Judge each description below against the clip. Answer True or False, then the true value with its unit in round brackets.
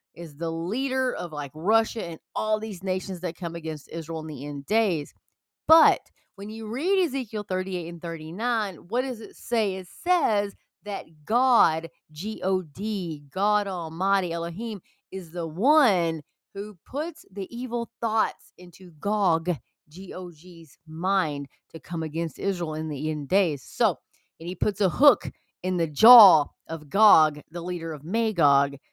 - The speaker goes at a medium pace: True (155 wpm)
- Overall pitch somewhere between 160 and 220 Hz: True (185 Hz)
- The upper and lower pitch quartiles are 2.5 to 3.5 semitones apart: False (4.9 semitones)